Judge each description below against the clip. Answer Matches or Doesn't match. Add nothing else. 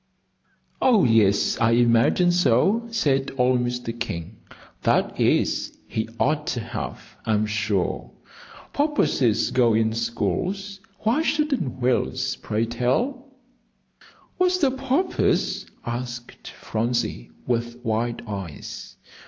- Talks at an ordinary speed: Doesn't match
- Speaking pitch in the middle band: Doesn't match